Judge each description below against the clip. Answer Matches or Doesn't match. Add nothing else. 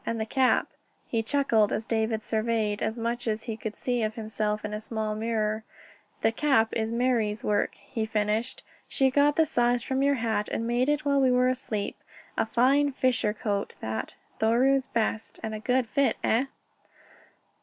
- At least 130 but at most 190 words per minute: Matches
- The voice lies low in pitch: Doesn't match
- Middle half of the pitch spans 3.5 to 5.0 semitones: Doesn't match